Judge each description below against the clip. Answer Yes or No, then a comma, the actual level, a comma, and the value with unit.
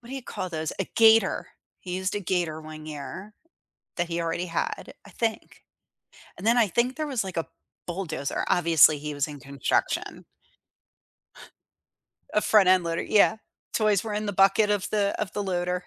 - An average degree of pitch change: Yes, average, 4.3 semitones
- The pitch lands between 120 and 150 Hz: No, medium, 185 Hz